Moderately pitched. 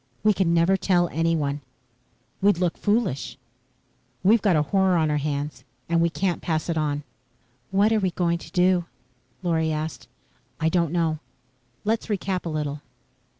Yes: medium, 170 Hz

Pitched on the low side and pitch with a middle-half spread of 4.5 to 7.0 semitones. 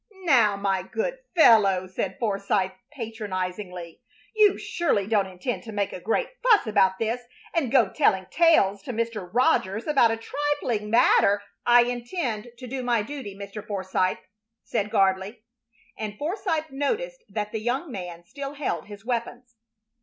No: high, 225 Hz; wide, 5.4 semitones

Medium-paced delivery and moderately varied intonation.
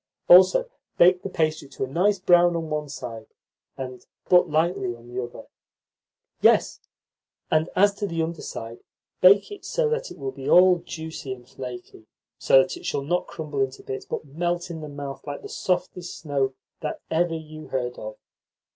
Yes: average, 180 wpm; average, 4.9 semitones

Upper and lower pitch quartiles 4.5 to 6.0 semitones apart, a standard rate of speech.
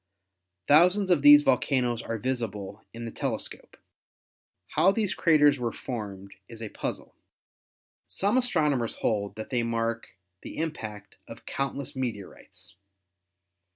No: average, 4.9 semitones; slow, 125 wpm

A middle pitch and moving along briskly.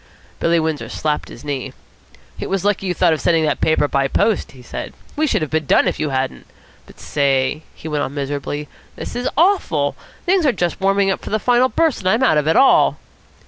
Yes: medium, 160 Hz; fast, 225 wpm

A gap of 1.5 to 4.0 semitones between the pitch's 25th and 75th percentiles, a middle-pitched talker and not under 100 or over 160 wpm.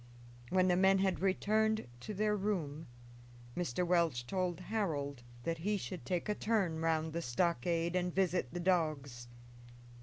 Yes: average, 3.2 semitones; medium, 175 Hz; average, 150 wpm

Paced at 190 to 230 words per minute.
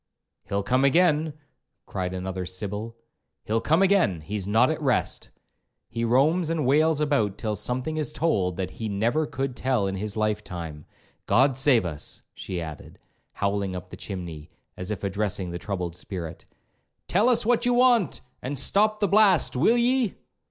No: average, 165 wpm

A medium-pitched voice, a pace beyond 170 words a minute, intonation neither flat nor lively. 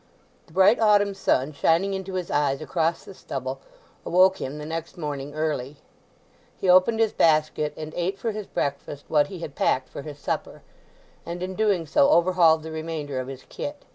Yes: medium, 160 Hz; average, 185 wpm; average, 4.4 semitones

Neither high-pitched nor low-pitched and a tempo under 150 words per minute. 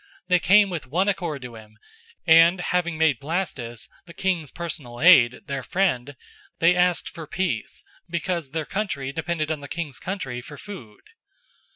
No: medium, 160 Hz; average, 160 wpm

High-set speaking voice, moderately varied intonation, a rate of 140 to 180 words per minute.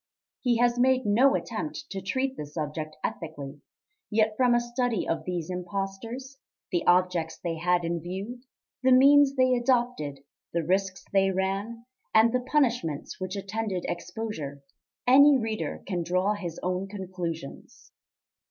No: high, 195 Hz; wide, 5.7 semitones; average, 145 wpm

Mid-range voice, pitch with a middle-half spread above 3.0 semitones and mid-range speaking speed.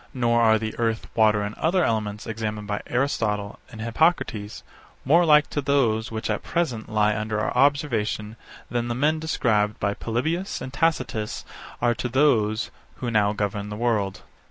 No: low, 115 Hz; average, 4.0 semitones; average, 165 wpm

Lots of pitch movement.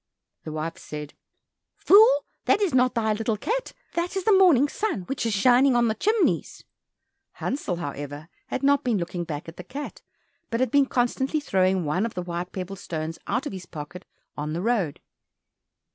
Yes: wide, 8.4 semitones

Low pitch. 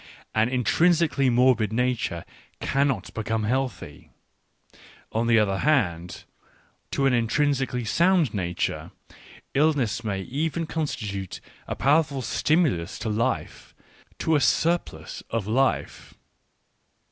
Yes: low, 125 Hz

